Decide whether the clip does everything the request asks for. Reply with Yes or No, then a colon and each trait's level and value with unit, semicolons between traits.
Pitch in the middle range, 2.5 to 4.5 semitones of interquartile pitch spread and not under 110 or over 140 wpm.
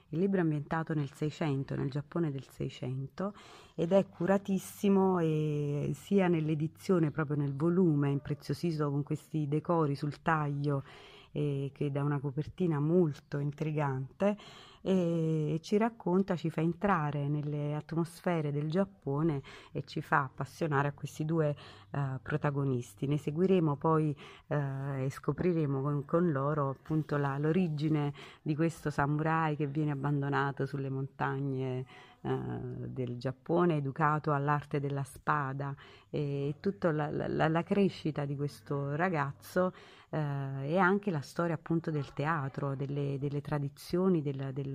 Yes: medium, 150 Hz; average, 2.8 semitones; average, 135 wpm